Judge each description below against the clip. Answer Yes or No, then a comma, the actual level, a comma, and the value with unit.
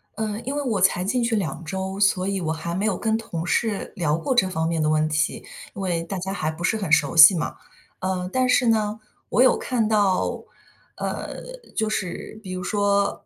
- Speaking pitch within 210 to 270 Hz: No, high, 190 Hz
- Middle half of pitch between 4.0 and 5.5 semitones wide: Yes, average, 4.3 semitones